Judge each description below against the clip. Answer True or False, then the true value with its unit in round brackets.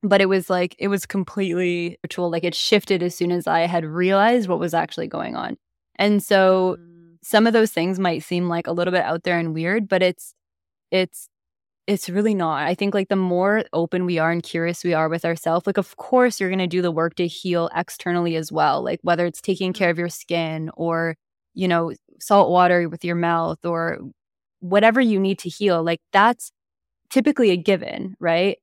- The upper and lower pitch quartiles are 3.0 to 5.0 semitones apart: False (2.6 semitones)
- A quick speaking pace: True (210 wpm)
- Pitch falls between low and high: True (175 Hz)